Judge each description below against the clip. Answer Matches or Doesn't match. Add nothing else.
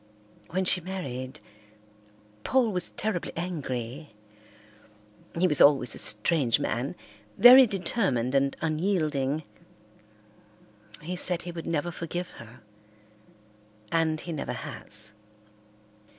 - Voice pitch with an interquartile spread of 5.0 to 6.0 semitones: Matches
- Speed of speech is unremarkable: Doesn't match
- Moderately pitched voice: Matches